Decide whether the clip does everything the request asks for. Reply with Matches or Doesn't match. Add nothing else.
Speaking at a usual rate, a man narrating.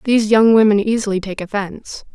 Doesn't match